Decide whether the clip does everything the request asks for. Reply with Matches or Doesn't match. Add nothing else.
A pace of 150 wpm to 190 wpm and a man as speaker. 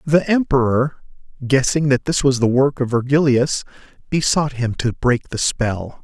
Matches